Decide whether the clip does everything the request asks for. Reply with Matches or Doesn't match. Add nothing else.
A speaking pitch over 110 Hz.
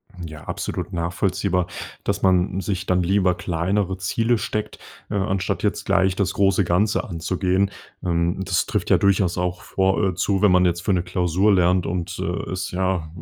Doesn't match